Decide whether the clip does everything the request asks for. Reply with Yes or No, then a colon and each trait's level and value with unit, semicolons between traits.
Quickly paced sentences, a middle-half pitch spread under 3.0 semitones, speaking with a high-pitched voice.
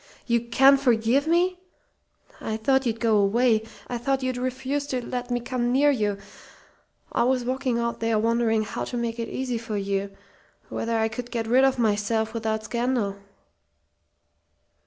No: average, 165 wpm; narrow, 2.6 semitones; high, 235 Hz